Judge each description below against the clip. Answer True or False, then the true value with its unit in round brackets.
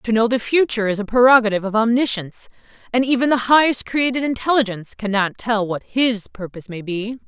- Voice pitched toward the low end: False (230 Hz)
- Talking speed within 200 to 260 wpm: False (180 wpm)